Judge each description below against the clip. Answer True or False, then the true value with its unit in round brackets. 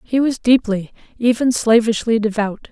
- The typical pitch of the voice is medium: False (230 Hz)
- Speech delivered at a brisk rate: False (135 wpm)